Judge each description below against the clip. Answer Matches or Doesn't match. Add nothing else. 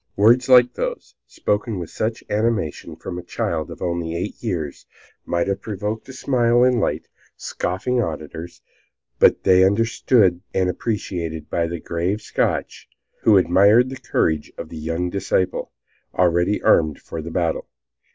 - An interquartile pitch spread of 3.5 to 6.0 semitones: Matches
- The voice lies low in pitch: Matches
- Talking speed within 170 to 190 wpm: Doesn't match